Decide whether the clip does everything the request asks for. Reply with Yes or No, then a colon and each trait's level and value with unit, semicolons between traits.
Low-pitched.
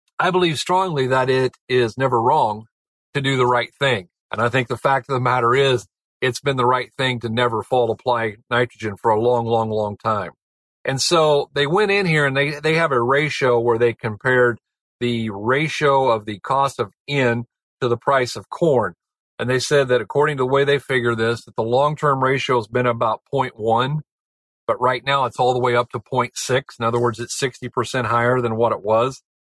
Yes: low, 125 Hz